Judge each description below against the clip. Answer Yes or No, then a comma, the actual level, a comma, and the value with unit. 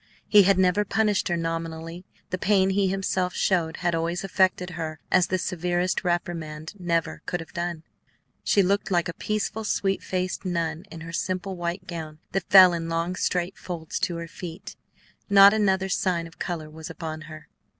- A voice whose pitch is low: No, medium, 175 Hz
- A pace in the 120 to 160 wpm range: No, average, 180 wpm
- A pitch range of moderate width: No, narrow, 2.3 semitones